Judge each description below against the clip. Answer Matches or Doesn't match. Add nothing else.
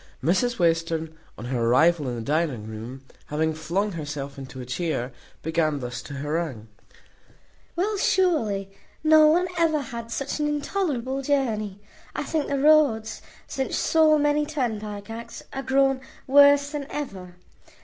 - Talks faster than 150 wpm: Doesn't match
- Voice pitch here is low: Doesn't match